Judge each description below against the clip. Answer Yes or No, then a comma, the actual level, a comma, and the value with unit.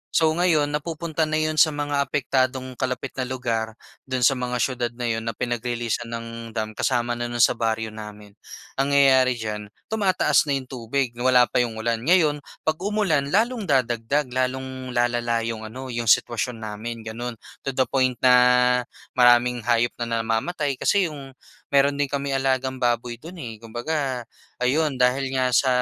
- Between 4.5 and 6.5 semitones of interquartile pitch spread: No, average, 3.1 semitones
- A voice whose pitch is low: Yes, low, 125 Hz